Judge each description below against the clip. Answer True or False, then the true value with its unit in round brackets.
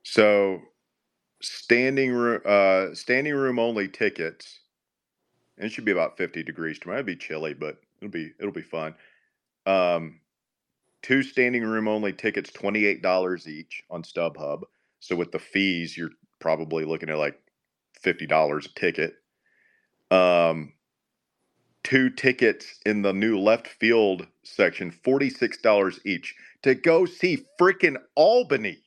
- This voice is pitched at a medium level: False (100 Hz)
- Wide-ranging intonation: True (7.1 semitones)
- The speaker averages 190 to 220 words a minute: False (140 wpm)